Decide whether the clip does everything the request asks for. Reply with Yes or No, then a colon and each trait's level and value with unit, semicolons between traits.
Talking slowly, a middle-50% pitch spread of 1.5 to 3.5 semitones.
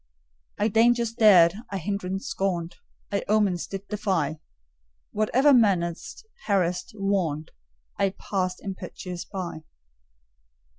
Yes: slow, 100 wpm; average, 3.0 semitones